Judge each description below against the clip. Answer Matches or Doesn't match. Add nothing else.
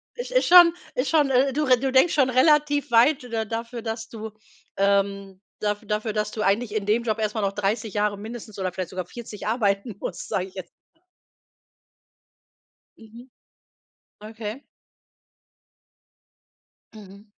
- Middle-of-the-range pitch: Doesn't match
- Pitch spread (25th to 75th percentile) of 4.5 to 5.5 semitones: Doesn't match